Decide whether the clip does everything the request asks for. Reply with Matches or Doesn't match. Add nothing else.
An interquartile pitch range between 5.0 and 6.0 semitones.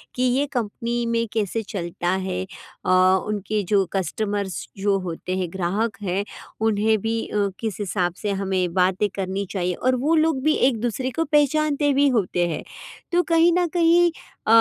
Matches